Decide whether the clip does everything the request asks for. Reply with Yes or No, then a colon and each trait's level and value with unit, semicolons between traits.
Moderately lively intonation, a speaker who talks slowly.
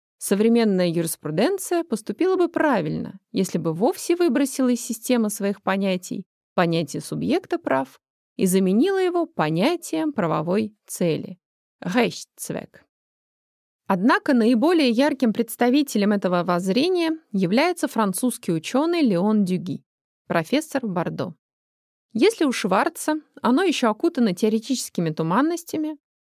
No: wide, 8.4 semitones; slow, 100 wpm